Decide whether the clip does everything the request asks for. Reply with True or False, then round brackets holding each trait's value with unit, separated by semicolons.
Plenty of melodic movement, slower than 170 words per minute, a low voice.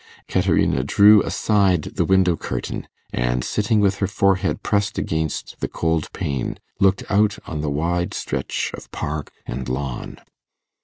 True (5.9 semitones; 145 wpm; 85 Hz)